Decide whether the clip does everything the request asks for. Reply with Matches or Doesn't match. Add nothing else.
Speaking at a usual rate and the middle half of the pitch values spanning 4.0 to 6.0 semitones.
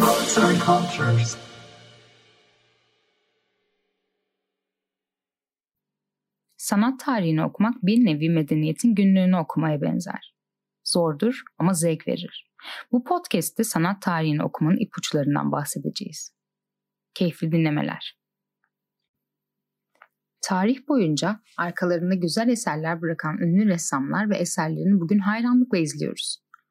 Doesn't match